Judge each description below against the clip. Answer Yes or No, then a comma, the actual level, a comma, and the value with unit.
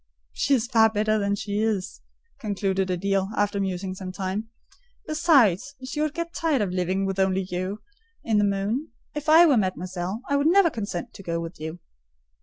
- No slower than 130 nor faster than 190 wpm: Yes, average, 185 wpm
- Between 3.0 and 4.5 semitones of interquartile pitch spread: No, average, 5.2 semitones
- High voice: Yes, high, 200 Hz